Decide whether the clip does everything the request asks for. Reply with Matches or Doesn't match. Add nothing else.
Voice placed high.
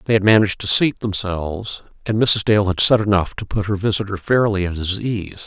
Doesn't match